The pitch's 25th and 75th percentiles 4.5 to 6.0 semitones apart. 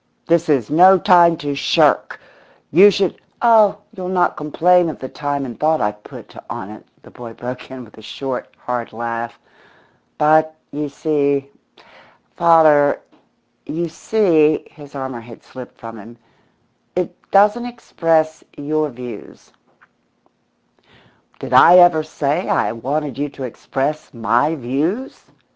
Yes: average, 5.0 semitones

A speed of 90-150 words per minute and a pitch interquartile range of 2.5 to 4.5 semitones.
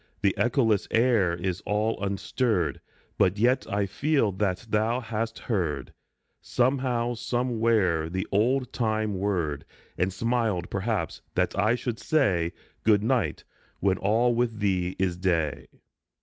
Yes: slow, 135 wpm; average, 4.1 semitones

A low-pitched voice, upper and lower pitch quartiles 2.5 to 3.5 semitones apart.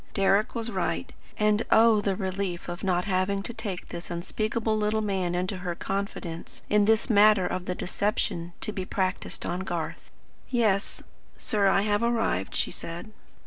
No: high, 195 Hz; average, 2.9 semitones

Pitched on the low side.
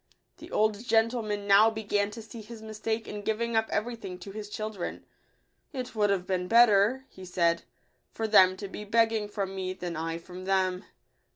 No: high, 210 Hz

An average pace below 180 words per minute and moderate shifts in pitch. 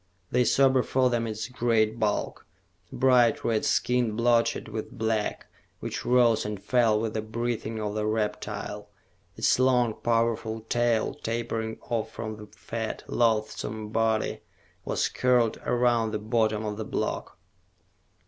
No: average, 140 wpm; narrow, 1.7 semitones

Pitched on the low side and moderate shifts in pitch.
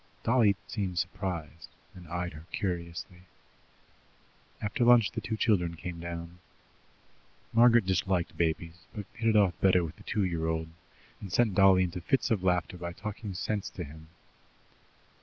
Yes: very low, 90 Hz; average, 3.4 semitones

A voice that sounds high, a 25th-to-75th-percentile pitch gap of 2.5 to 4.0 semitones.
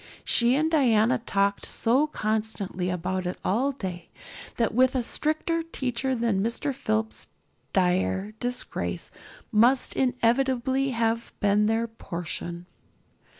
No: high, 230 Hz; average, 4.4 semitones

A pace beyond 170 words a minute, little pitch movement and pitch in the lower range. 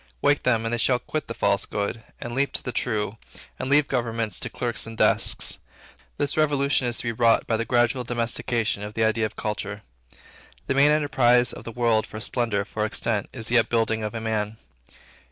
Yes: fast, 205 wpm; narrow, 2.1 semitones; low, 115 Hz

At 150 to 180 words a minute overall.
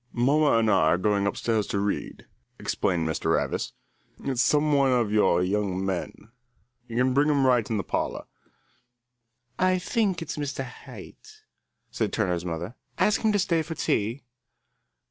Yes: average, 160 wpm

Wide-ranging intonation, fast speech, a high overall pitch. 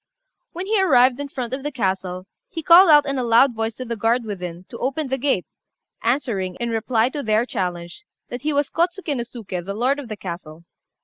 Yes: wide, 5.8 semitones; fast, 215 wpm; high, 240 Hz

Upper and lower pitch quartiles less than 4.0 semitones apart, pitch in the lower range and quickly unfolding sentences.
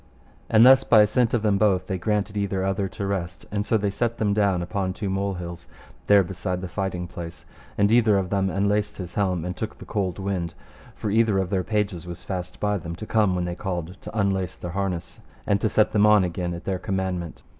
Yes: narrow, 2.4 semitones; very low, 95 Hz; fast, 230 wpm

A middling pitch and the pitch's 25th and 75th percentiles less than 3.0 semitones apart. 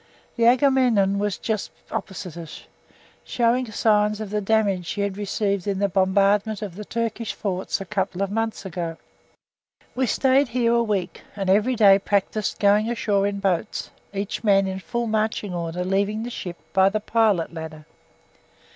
No: high, 205 Hz; narrow, 2.5 semitones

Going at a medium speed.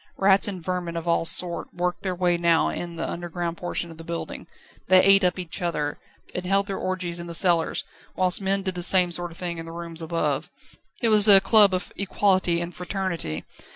No: fast, 215 wpm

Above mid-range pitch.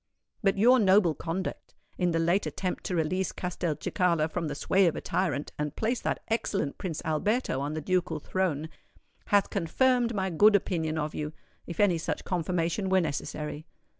No: medium, 175 Hz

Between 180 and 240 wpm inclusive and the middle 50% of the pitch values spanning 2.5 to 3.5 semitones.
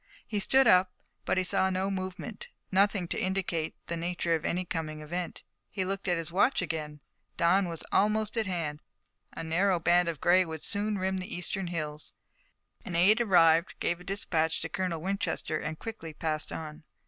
Yes: average, 185 wpm; average, 2.9 semitones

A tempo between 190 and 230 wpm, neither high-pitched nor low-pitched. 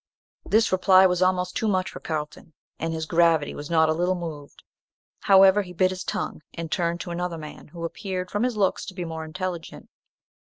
Yes: average, 200 wpm; medium, 180 Hz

